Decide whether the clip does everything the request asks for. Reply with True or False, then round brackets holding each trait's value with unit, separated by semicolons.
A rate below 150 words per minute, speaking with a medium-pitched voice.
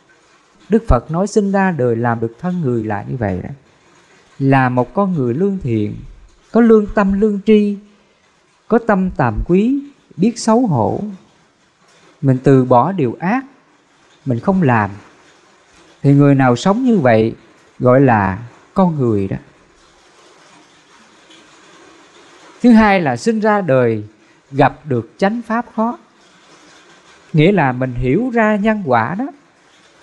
True (140 wpm; 175 Hz)